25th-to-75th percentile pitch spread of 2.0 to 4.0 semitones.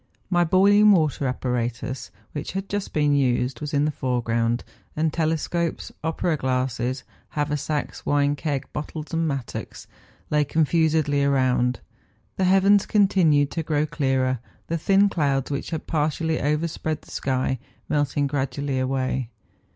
Yes: average, 3.5 semitones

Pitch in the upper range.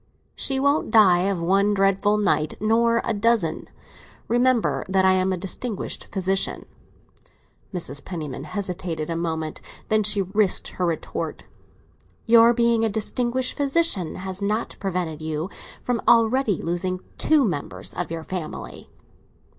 Yes: high, 195 Hz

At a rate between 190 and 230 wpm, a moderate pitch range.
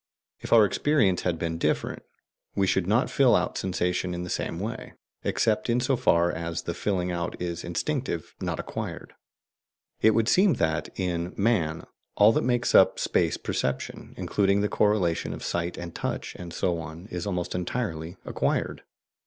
No: average, 170 wpm; average, 4.1 semitones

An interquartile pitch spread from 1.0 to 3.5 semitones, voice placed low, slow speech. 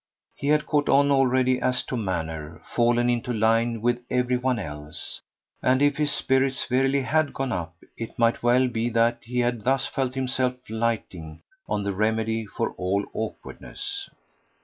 No: average, 2.9 semitones; low, 120 Hz; average, 165 wpm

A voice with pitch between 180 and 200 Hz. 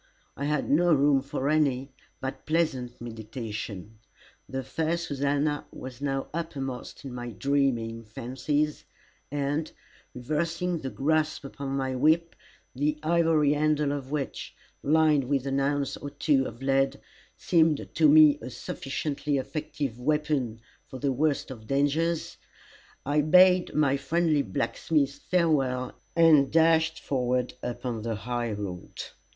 No: medium, 140 Hz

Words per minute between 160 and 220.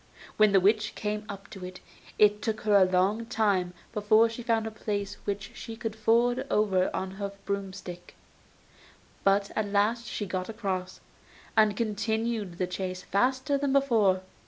Yes: average, 165 wpm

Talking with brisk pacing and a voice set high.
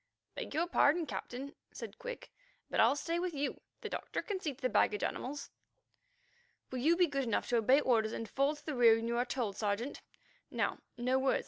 Yes: fast, 210 wpm; very high, 270 Hz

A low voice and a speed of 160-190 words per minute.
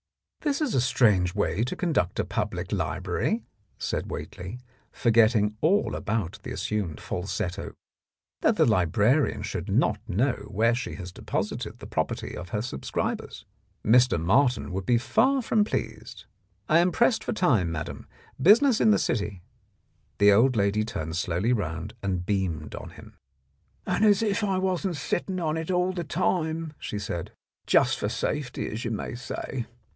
Yes: low, 115 Hz; average, 165 wpm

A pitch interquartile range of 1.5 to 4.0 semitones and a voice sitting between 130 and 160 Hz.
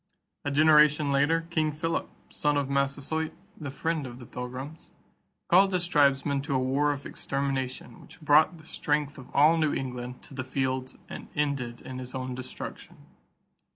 Yes: average, 2.7 semitones; medium, 140 Hz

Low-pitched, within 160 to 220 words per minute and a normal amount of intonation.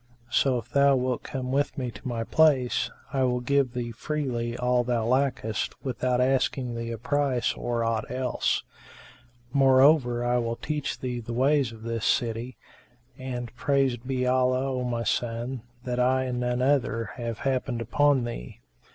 No: low, 125 Hz; average, 165 wpm; narrow, 1.9 semitones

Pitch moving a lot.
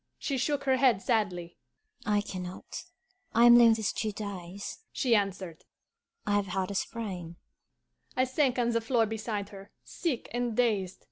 No: average, 3.7 semitones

